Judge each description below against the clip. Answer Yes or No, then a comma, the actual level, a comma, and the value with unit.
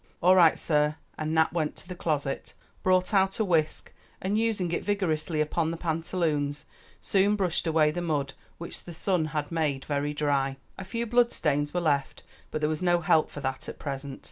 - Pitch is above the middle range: No, medium, 160 Hz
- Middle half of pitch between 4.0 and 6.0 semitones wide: No, average, 3.5 semitones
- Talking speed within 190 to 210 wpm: Yes, average, 195 wpm